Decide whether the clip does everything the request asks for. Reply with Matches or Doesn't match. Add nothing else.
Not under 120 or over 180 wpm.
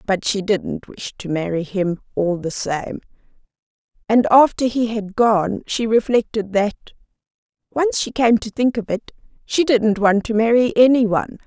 Matches